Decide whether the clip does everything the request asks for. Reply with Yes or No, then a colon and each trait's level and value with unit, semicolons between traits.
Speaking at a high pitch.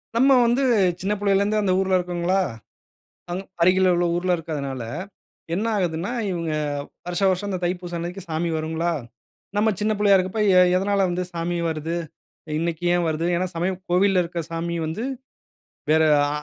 No: medium, 180 Hz